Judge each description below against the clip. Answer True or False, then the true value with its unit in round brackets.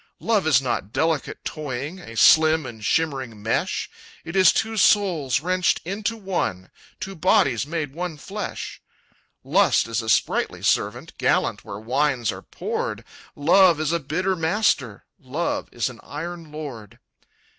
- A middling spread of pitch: False (6.1 semitones)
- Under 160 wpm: True (145 wpm)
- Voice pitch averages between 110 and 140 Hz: False (155 Hz)